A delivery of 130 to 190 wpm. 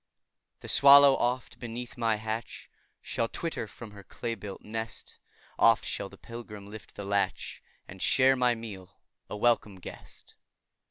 Yes: average, 150 wpm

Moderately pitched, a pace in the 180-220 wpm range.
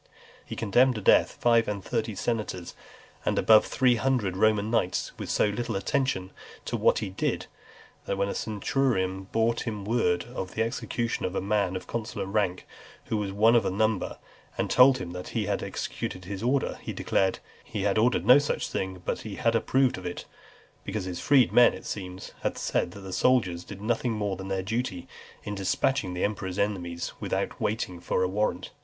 No: low, 105 Hz; average, 195 wpm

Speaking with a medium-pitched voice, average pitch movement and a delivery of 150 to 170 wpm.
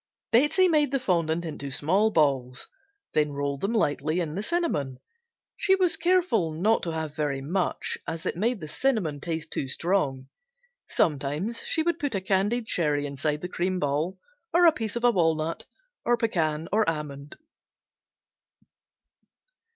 No: medium, 170 Hz; wide, 7.1 semitones; average, 155 wpm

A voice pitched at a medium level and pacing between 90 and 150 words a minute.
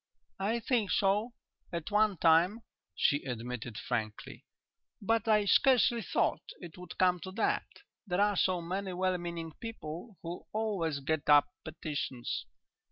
Yes: medium, 180 Hz; average, 140 wpm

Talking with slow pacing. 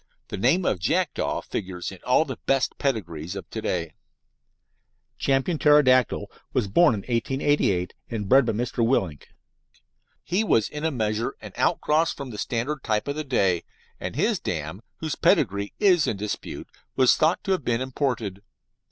No: average, 165 wpm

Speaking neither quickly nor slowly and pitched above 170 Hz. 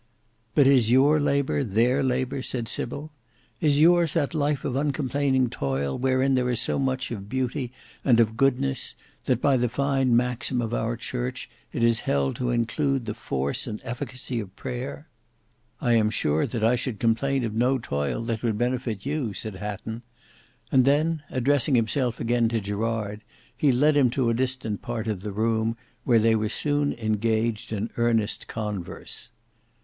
No: average, 170 wpm; low, 120 Hz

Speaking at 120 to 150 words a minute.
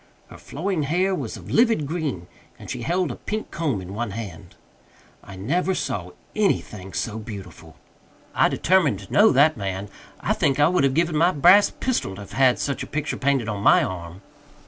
No: average, 190 wpm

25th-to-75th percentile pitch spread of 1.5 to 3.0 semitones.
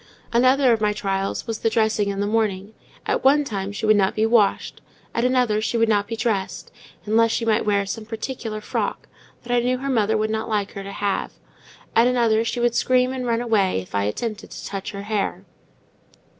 Yes: average, 2.7 semitones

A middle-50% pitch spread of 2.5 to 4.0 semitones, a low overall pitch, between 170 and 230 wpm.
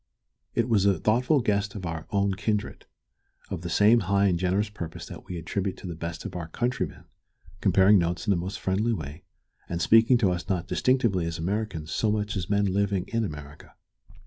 Yes: average, 3.5 semitones; low, 100 Hz; average, 200 wpm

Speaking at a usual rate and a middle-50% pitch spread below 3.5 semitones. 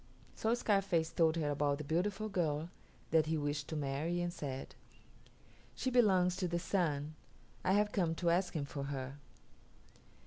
No: average, 165 wpm; average, 4.1 semitones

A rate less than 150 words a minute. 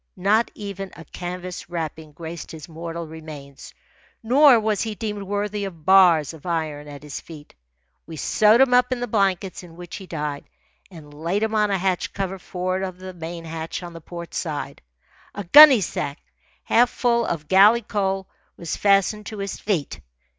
No: average, 175 wpm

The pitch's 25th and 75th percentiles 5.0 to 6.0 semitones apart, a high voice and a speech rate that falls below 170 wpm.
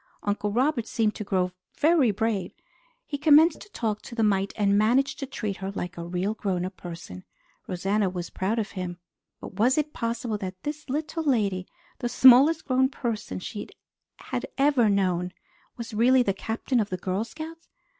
No: average, 5.3 semitones; high, 215 Hz; average, 180 wpm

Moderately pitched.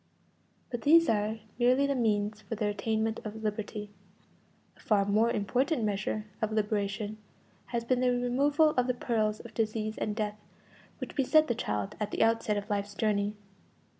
No: high, 220 Hz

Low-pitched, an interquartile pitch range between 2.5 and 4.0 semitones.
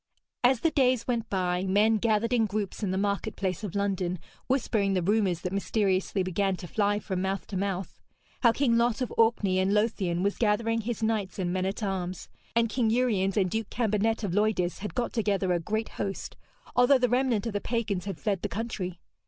No: high, 205 Hz; average, 3.1 semitones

